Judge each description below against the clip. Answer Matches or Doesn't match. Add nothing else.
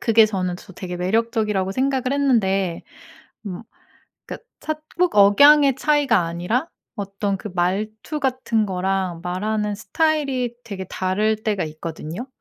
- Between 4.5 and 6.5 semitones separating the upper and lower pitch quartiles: Matches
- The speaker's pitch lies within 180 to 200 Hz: Doesn't match